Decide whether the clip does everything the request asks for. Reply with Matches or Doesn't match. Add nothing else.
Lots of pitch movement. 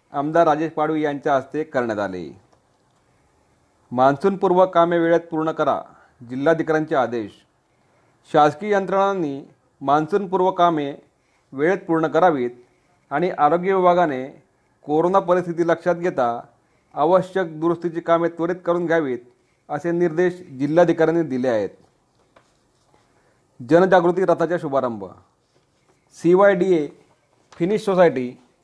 Doesn't match